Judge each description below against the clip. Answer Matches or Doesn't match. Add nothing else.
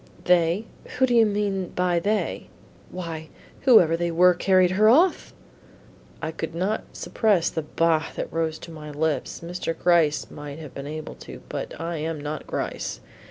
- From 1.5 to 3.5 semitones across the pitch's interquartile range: Matches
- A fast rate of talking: Doesn't match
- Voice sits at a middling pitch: Matches